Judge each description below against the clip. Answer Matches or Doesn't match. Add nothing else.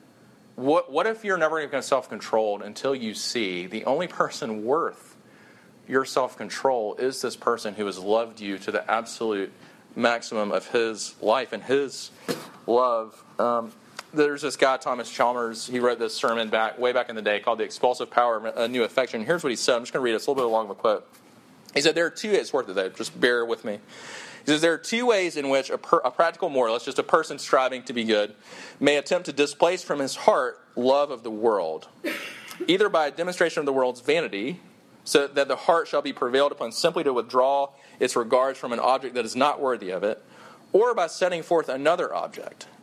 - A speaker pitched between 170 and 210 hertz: Doesn't match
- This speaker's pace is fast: Matches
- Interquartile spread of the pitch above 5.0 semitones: Matches